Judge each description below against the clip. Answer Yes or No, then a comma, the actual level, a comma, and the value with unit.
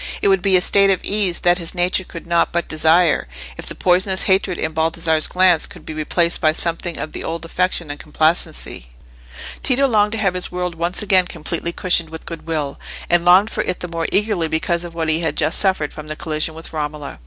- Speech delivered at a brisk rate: Yes, fast, 220 wpm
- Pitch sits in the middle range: Yes, medium, 170 Hz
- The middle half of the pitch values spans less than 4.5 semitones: Yes, narrow, 2.4 semitones